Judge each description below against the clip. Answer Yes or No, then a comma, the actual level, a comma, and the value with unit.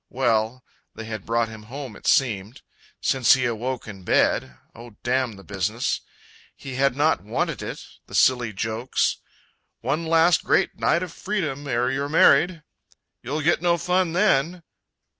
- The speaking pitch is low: Yes, low, 130 Hz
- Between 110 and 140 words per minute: No, average, 155 wpm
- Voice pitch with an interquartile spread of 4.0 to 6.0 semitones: Yes, wide, 5.5 semitones